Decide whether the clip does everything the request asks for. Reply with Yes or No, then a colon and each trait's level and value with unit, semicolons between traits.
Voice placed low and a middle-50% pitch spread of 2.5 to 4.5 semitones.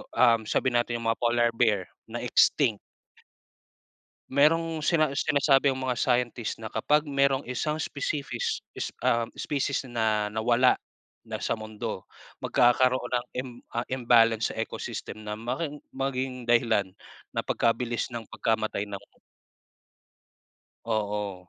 Yes: low, 120 Hz; average, 2.9 semitones